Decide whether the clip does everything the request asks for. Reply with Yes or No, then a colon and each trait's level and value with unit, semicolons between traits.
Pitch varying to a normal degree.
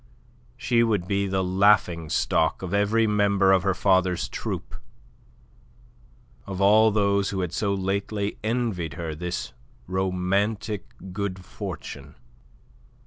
No: narrow, 2.0 semitones